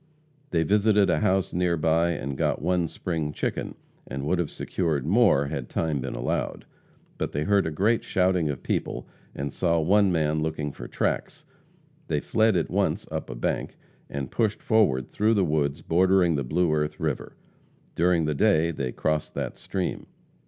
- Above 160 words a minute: Yes, average, 175 wpm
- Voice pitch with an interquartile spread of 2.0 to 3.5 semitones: No, average, 3.9 semitones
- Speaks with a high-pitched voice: No, very low, 80 Hz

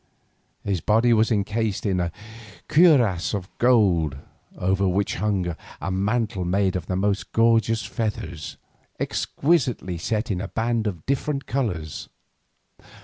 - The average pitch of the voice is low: Yes, low, 105 Hz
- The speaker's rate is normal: No, slow, 125 wpm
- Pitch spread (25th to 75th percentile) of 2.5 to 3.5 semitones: No, average, 3.9 semitones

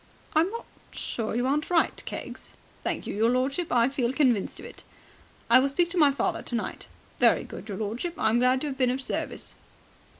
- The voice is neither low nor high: No, very high, 260 Hz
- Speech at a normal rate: No, fast, 210 wpm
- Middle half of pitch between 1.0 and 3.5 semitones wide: No, average, 4.1 semitones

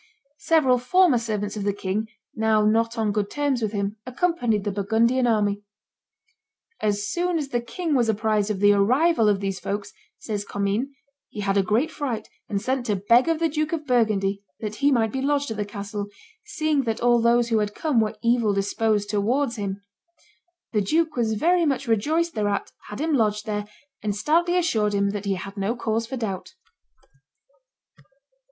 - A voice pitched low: No, high, 220 Hz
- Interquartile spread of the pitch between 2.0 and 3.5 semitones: No, average, 4.4 semitones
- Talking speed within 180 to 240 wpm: Yes, average, 185 wpm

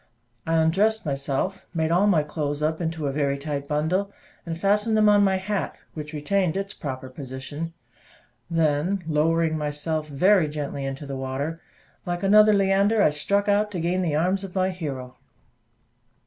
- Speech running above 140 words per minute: Yes, average, 165 wpm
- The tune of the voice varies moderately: Yes, average, 4.8 semitones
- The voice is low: No, medium, 165 Hz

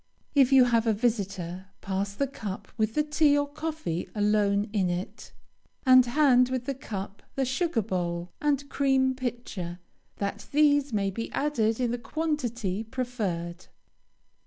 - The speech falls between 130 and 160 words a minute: Yes, average, 150 wpm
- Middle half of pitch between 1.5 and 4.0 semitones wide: No, wide, 5.6 semitones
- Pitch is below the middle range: No, high, 240 Hz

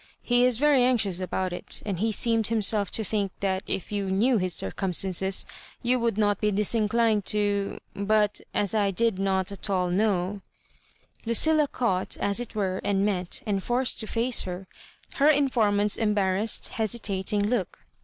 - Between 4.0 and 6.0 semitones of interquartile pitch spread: No, average, 3.0 semitones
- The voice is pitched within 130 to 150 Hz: No, high, 210 Hz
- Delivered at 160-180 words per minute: Yes, average, 165 wpm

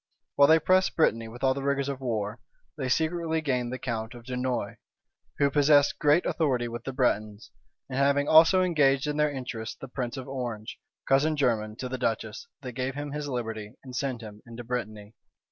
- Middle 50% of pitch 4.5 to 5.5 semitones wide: No, average, 3.4 semitones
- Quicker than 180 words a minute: Yes, average, 195 wpm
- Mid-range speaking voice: No, low, 130 Hz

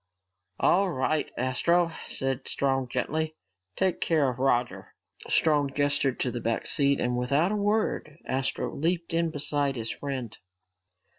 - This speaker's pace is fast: No, average, 140 wpm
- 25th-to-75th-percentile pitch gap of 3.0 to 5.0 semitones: Yes, average, 4.0 semitones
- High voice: No, medium, 140 Hz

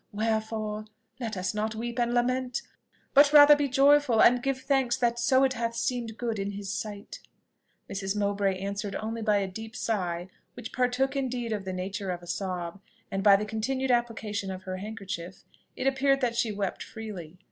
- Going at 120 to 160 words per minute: No, average, 185 wpm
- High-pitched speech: Yes, high, 220 Hz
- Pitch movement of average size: Yes, average, 3.8 semitones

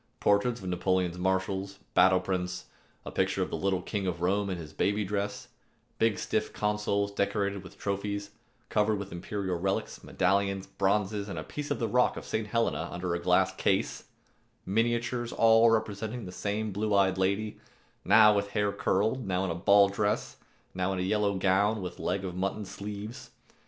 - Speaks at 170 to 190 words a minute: Yes, average, 175 wpm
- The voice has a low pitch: Yes, low, 100 Hz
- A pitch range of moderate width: No, narrow, 2.0 semitones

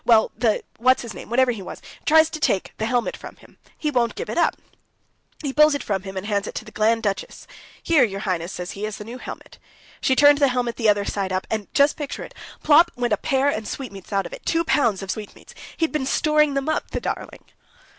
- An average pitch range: No, wide, 5.8 semitones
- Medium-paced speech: No, fast, 235 wpm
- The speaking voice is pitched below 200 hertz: No, high, 235 Hz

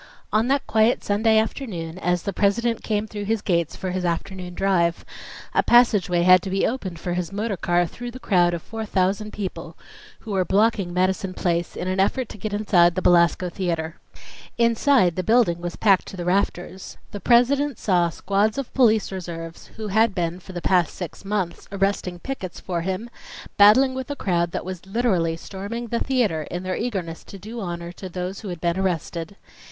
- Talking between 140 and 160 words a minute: No, average, 195 wpm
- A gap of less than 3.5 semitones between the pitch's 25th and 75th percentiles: No, average, 3.8 semitones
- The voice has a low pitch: No, high, 190 Hz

